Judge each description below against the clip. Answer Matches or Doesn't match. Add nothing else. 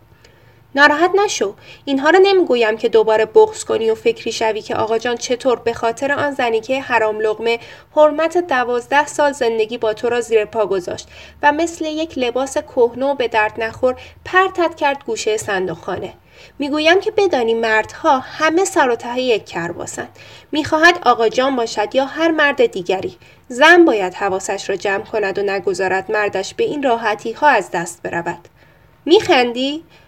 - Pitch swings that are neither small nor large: Doesn't match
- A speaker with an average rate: Doesn't match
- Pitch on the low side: Doesn't match